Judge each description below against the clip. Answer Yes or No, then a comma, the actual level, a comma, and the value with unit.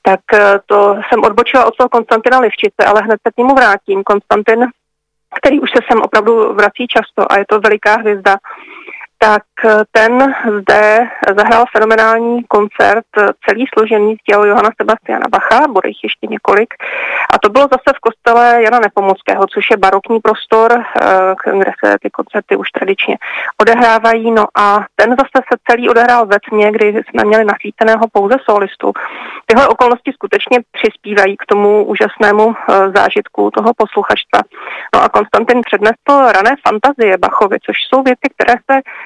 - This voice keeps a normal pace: Yes, average, 150 wpm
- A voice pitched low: No, high, 225 Hz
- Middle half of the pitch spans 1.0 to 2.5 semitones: No, average, 2.9 semitones